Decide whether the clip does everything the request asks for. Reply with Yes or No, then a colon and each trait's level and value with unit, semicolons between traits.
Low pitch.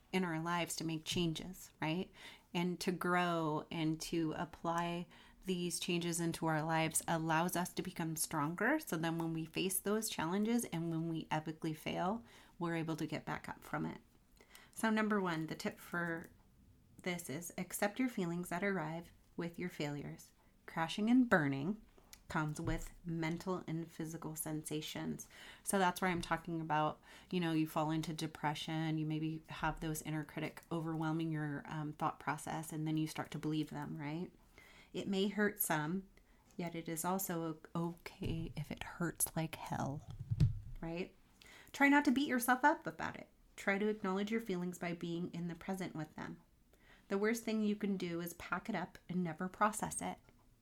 No: medium, 170 Hz